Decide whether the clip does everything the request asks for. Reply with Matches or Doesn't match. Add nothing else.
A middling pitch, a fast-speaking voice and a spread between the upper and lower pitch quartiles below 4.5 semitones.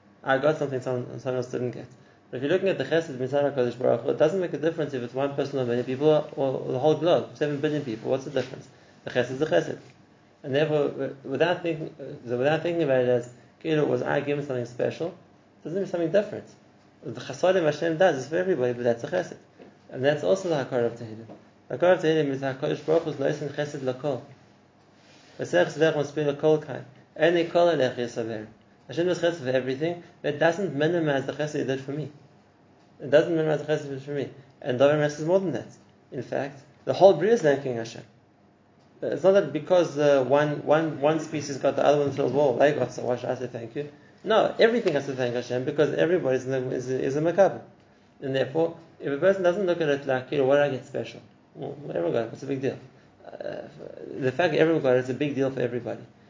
Matches